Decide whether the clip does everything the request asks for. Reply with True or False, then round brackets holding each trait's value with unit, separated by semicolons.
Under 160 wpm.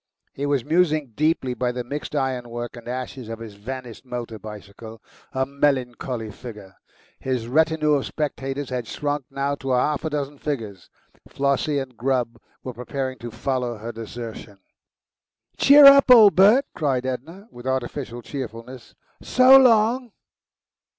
True (145 wpm)